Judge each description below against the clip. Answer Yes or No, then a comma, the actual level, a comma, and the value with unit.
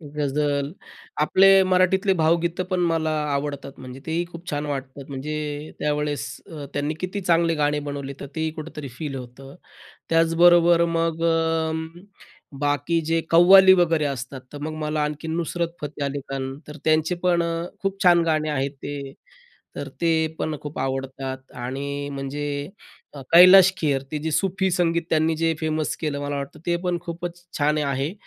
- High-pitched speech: No, medium, 155 Hz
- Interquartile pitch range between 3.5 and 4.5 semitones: No, average, 2.9 semitones